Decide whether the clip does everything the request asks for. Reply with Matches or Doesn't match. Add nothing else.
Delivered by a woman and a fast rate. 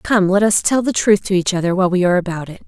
Matches